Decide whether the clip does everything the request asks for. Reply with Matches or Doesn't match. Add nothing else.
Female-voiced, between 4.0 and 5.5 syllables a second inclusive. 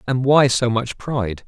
Doesn't match